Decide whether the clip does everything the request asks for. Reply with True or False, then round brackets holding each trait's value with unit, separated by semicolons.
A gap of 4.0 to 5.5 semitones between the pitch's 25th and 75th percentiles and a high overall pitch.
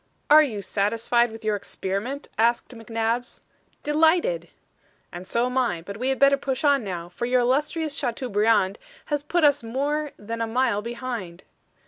True (4.5 semitones; 240 Hz)